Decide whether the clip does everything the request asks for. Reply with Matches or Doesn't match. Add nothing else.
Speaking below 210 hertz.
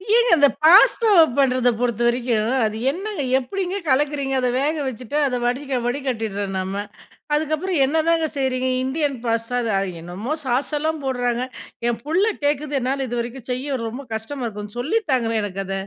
Doesn't match